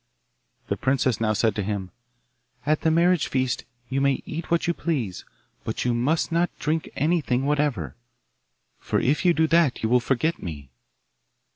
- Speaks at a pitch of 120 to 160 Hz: Yes, low, 135 Hz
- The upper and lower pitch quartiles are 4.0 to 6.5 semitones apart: Yes, wide, 5.6 semitones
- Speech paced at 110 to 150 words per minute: No, average, 165 wpm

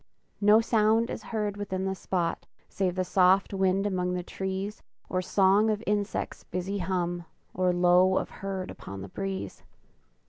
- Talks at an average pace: Yes, average, 160 wpm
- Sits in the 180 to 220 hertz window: Yes, high, 190 Hz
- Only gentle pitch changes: Yes, narrow, 2.0 semitones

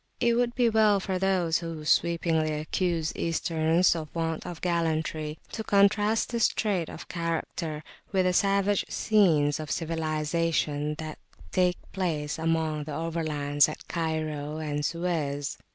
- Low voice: No, medium, 165 Hz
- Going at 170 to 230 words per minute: No, slow, 135 wpm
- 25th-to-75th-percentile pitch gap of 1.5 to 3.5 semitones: Yes, average, 3.0 semitones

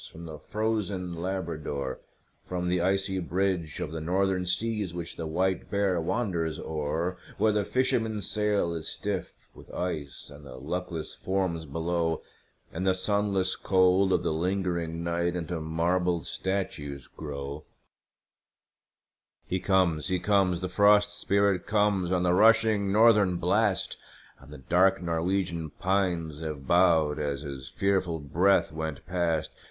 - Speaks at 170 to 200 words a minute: No, average, 140 wpm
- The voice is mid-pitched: No, very low, 90 Hz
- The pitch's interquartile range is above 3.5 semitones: No, average, 3.2 semitones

